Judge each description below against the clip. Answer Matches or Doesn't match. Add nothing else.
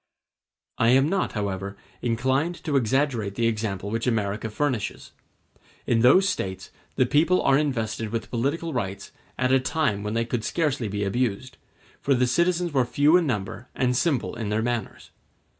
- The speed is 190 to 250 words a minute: Doesn't match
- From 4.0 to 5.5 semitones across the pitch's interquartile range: Matches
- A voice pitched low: Matches